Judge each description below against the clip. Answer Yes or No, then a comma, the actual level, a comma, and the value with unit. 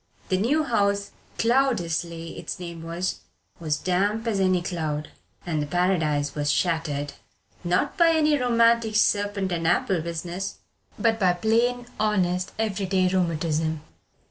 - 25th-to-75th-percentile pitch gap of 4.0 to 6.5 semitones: Yes, average, 4.6 semitones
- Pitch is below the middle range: No, medium, 185 Hz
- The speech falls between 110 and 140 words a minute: Yes, slow, 135 wpm